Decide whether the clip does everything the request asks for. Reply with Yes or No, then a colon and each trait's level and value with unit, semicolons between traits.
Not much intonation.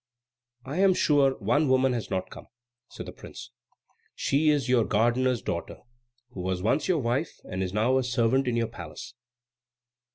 No: average, 4.1 semitones